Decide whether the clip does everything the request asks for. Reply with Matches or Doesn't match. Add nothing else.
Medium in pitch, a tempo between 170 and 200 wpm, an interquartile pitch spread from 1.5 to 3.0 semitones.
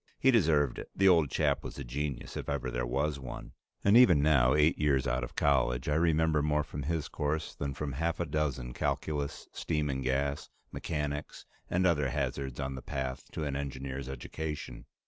Doesn't match